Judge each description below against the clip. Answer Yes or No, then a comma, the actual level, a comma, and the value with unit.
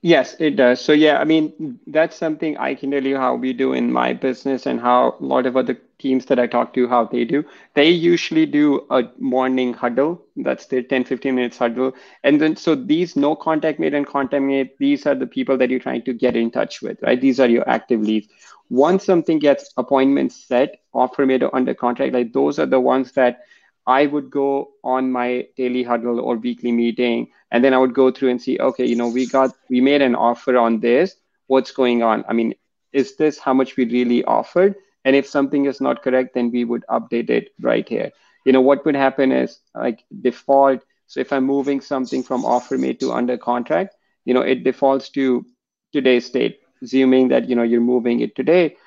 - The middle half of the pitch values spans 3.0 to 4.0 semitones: No, narrow, 2.4 semitones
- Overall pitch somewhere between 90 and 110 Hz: No, low, 130 Hz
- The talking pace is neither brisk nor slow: No, fast, 215 wpm